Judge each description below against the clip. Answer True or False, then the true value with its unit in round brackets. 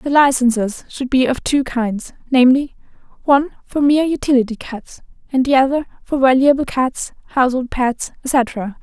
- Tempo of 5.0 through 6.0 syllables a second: True (5.1 syllables/s)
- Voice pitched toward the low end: False (260 Hz)